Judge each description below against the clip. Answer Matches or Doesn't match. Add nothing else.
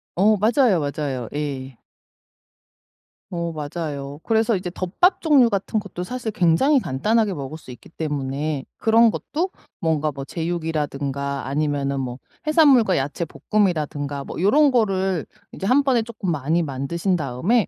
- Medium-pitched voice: Matches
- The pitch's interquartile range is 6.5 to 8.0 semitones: Matches